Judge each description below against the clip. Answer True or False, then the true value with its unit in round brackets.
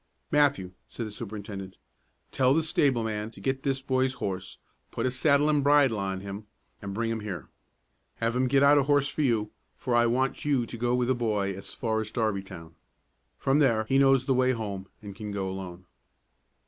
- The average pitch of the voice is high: False (115 Hz)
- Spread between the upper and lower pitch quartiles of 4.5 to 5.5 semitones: True (4.8 semitones)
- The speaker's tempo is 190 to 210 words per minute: True (200 wpm)